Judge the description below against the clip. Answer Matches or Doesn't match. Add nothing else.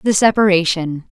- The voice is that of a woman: Matches